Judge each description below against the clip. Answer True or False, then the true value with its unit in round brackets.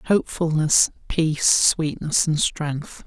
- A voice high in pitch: False (160 Hz)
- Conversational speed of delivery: False (100 wpm)